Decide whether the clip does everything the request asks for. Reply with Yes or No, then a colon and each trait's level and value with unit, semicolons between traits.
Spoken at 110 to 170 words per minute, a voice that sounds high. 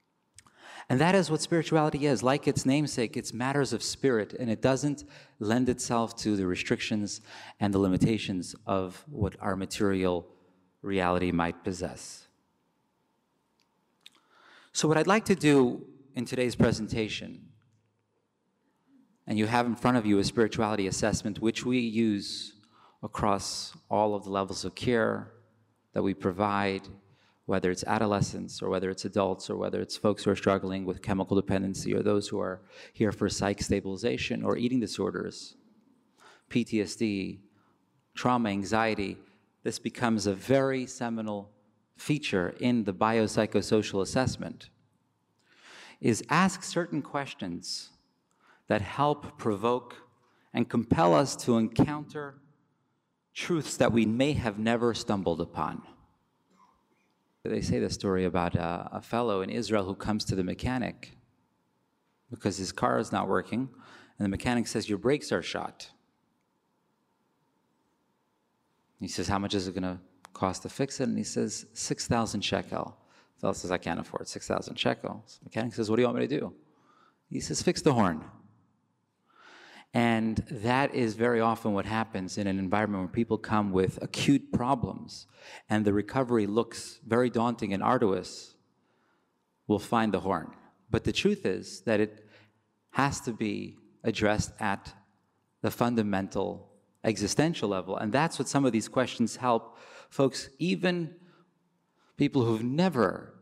No: average, 145 wpm; low, 110 Hz